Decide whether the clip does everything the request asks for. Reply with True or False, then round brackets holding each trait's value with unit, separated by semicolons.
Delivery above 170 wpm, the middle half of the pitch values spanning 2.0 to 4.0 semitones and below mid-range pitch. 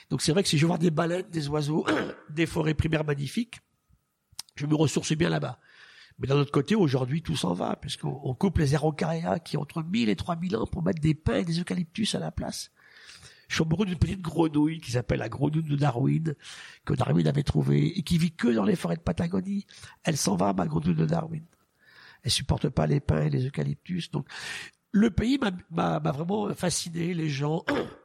False (215 wpm; 3.1 semitones; 165 Hz)